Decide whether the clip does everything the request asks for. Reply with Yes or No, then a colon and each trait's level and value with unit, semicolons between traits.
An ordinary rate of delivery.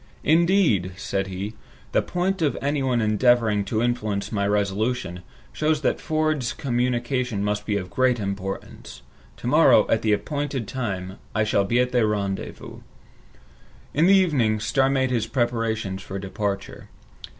Yes: average, 145 wpm